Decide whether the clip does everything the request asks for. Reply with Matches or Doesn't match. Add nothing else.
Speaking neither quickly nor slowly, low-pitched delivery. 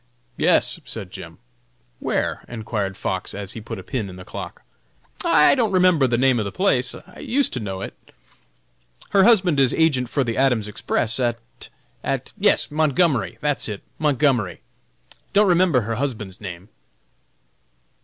Matches